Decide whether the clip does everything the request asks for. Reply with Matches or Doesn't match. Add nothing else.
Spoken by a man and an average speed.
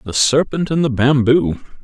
Matches